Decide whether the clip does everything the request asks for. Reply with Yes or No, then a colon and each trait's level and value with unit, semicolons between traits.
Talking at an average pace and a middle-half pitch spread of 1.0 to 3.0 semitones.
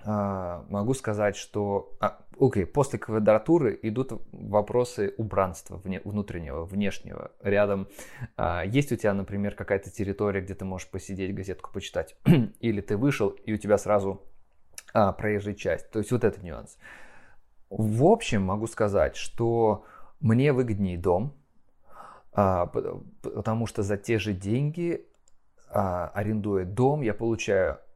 Yes: average, 135 wpm; narrow, 2.5 semitones